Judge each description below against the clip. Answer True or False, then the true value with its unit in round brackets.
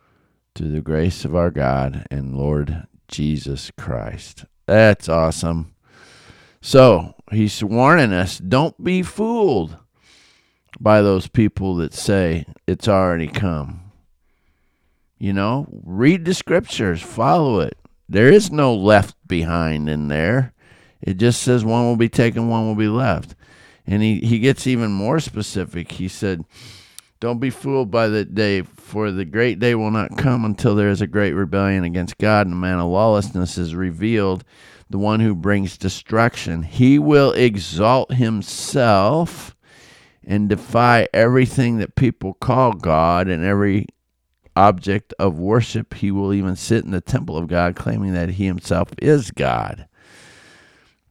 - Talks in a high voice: False (100 Hz)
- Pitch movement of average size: True (5.0 semitones)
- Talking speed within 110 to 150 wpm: True (145 wpm)